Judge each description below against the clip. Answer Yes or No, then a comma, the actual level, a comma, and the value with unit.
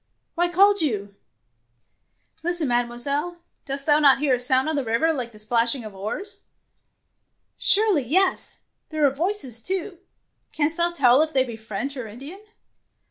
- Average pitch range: No, wide, 6.0 semitones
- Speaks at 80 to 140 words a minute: No, average, 170 wpm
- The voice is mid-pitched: No, very high, 280 Hz